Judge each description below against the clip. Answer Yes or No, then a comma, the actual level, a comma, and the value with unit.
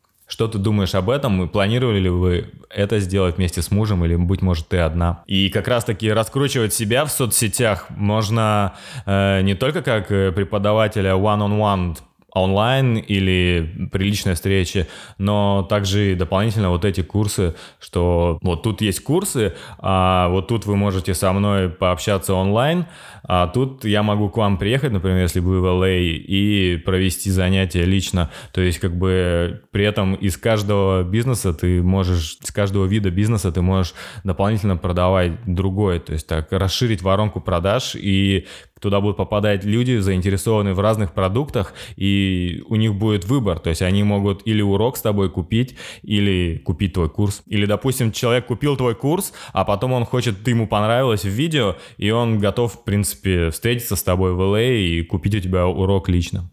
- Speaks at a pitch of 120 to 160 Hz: No, low, 100 Hz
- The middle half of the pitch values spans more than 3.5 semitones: No, average, 2.8 semitones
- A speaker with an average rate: No, fast, 170 wpm